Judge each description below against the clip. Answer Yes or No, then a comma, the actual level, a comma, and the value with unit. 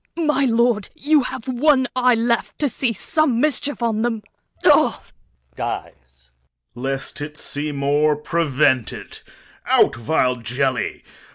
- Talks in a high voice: Yes, high, 215 Hz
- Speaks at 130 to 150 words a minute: Yes, average, 140 wpm